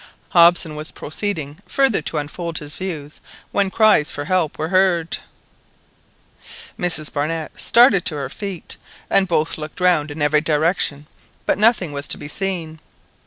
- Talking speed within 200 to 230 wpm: No, average, 150 wpm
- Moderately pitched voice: Yes, medium, 165 Hz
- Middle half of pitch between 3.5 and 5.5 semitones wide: Yes, average, 3.8 semitones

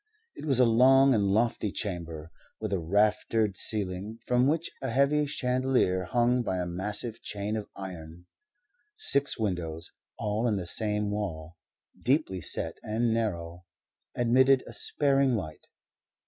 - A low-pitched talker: Yes, low, 105 Hz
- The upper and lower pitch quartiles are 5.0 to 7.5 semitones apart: Yes, average, 5.3 semitones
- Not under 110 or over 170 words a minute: Yes, average, 140 wpm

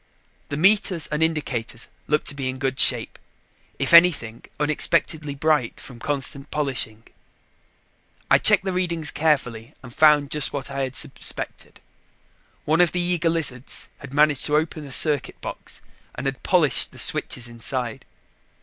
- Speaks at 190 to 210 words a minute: No, average, 150 wpm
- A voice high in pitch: No, medium, 145 Hz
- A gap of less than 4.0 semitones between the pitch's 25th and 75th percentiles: Yes, average, 3.5 semitones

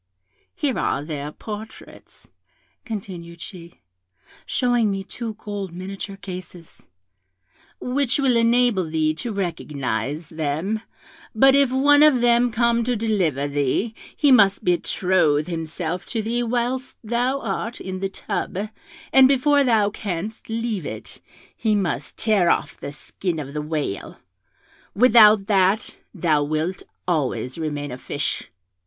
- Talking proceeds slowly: Yes, slow, 130 wpm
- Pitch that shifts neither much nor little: No, wide, 6.4 semitones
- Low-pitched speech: No, high, 195 Hz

